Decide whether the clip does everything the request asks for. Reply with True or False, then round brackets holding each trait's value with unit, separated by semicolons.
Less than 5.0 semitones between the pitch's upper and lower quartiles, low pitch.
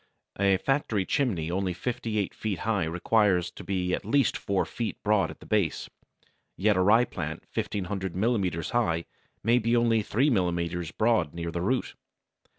True (4.3 semitones; 100 Hz)